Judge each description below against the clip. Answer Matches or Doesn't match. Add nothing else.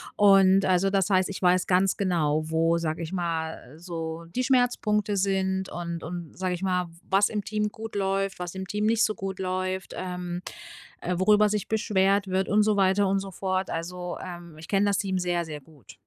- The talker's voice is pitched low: Doesn't match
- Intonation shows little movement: Matches